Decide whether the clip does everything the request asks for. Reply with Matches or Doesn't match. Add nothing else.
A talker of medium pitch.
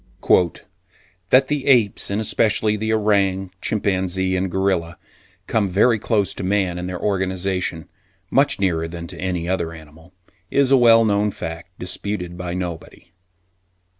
Doesn't match